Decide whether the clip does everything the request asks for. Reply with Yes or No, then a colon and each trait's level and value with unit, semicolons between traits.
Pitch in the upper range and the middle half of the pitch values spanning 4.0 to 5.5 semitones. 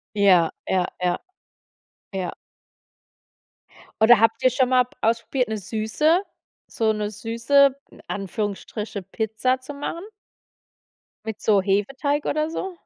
Yes: high, 225 Hz; average, 4.6 semitones